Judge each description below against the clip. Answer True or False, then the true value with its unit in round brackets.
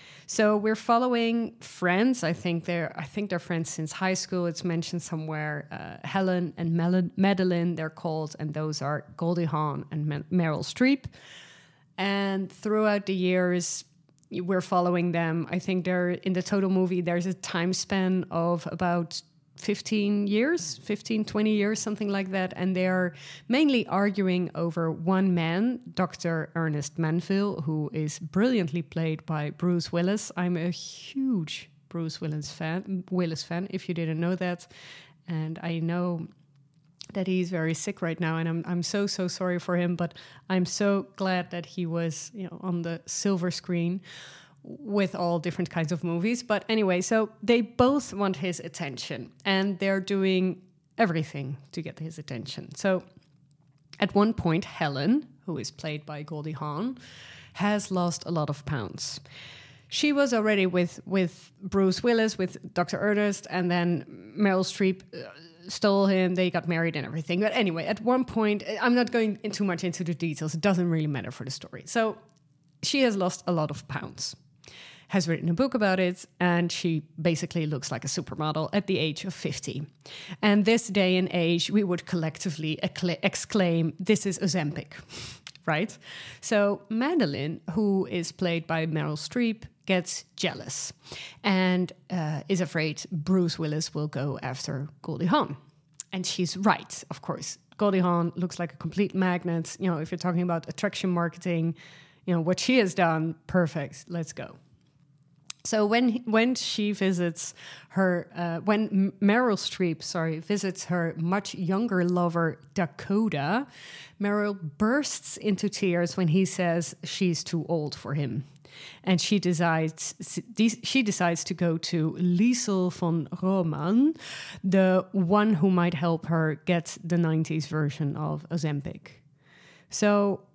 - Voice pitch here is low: False (175 Hz)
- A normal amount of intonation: True (3.3 semitones)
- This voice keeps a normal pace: True (160 wpm)